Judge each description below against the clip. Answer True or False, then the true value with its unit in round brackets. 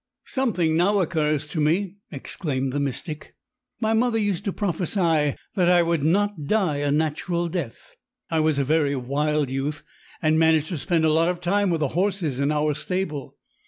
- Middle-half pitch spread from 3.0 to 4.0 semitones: True (3.5 semitones)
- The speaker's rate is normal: True (180 wpm)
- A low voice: False (160 Hz)